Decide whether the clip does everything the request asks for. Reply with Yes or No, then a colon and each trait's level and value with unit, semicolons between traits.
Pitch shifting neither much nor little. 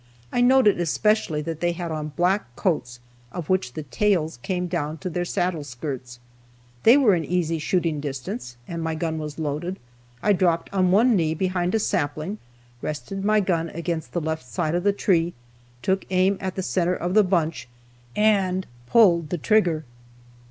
Yes: average, 3.4 semitones